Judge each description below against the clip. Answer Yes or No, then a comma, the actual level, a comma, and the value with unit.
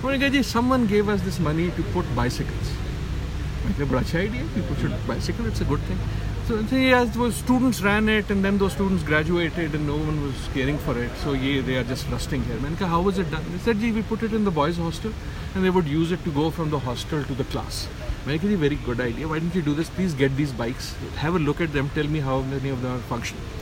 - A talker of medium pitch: Yes, medium, 150 Hz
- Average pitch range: No, wide, 6.9 semitones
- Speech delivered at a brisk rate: Yes, fast, 240 wpm